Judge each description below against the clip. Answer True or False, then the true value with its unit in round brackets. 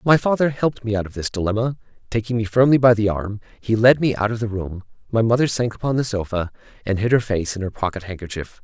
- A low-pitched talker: True (110 Hz)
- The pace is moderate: False (245 wpm)